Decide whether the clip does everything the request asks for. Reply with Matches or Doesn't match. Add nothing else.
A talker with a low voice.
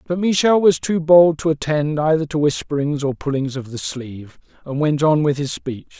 Doesn't match